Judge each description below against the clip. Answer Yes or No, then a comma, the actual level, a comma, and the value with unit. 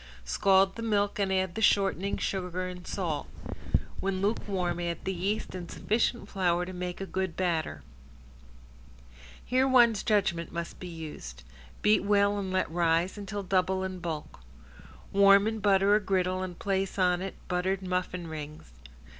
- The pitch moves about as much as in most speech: No, narrow, 2.2 semitones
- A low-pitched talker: No, high, 190 Hz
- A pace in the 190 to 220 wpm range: No, average, 155 wpm